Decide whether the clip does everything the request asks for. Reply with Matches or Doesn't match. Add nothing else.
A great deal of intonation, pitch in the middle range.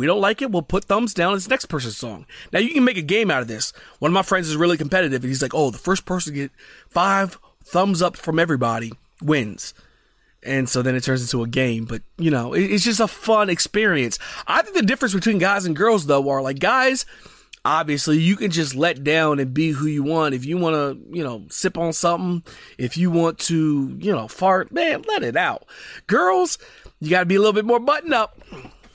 Matches